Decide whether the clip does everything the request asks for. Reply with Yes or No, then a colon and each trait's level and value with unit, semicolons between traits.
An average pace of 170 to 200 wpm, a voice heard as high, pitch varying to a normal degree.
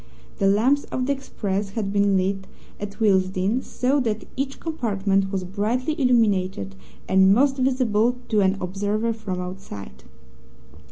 No: slow, 135 wpm; high, 205 Hz; average, 4.4 semitones